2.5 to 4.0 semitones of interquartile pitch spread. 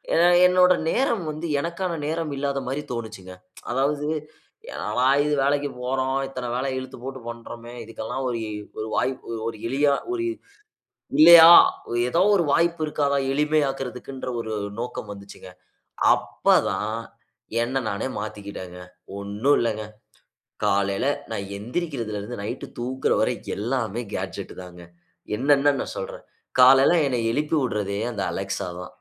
No: average, 4.8 semitones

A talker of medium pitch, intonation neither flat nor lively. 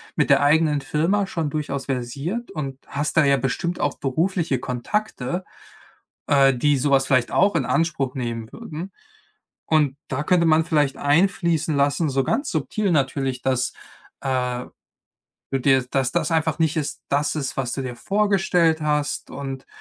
Yes: medium, 145 Hz; average, 3.5 semitones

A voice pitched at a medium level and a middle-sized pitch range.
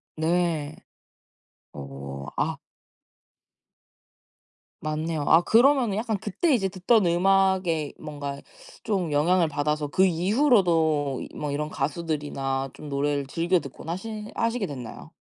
Yes: medium, 165 Hz; average, 4.8 semitones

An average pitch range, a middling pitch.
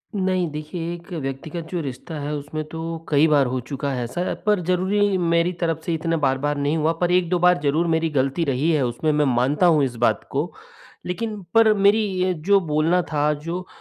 Yes: average, 3.7 semitones; medium, 160 Hz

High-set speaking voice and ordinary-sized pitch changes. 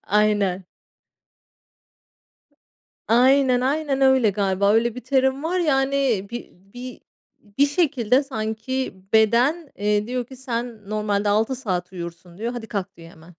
Yes: high, 235 Hz; average, 4.5 semitones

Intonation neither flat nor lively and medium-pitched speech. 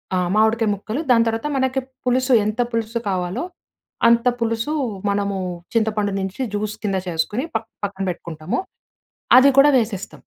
No: average, 3.3 semitones; high, 220 Hz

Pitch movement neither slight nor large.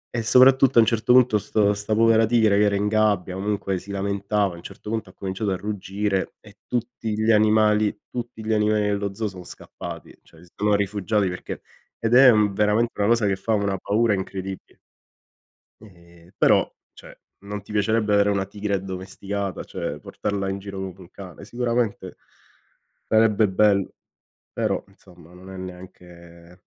No: narrow, 2.2 semitones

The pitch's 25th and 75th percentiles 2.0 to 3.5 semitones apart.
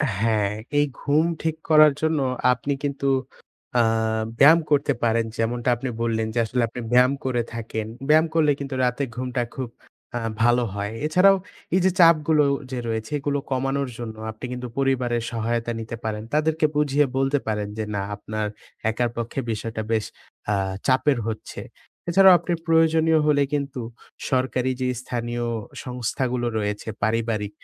No: average, 4.3 semitones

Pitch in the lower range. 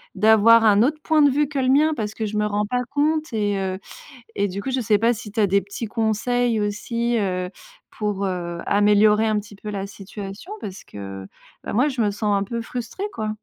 No: high, 215 Hz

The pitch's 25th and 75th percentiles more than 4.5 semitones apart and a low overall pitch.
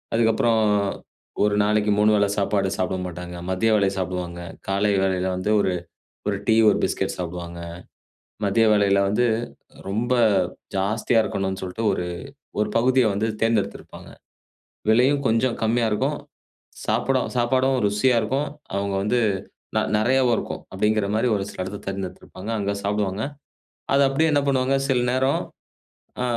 No: average, 3.8 semitones; low, 105 Hz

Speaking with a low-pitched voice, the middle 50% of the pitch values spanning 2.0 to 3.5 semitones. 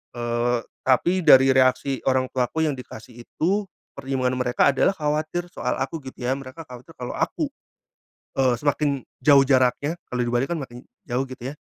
Yes: low, 130 Hz; average, 2.8 semitones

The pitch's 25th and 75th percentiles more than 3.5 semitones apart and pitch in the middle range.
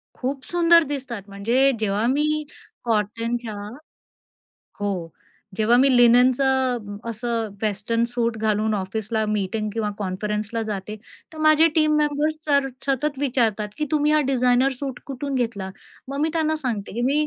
No: average, 4.7 semitones; high, 240 Hz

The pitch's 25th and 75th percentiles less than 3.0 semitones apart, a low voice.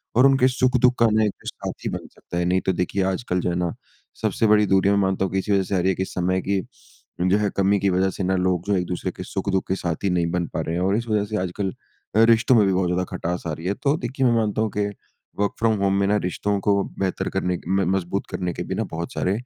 Yes: narrow, 2.5 semitones; very low, 95 Hz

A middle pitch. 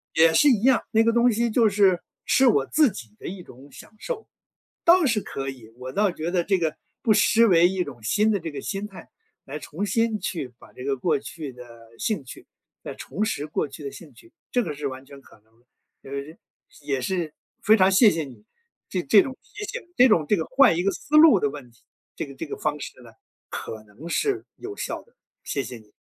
Yes: medium, 170 Hz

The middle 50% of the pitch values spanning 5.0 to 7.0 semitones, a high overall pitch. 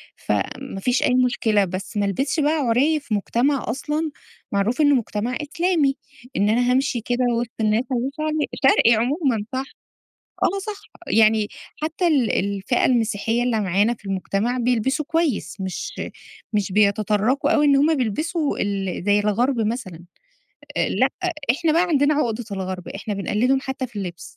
Yes: average, 5.3 semitones; high, 240 Hz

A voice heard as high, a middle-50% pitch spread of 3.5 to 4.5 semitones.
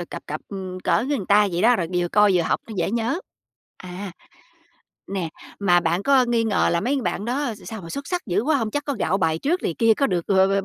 No: high, 205 Hz; average, 5.2 semitones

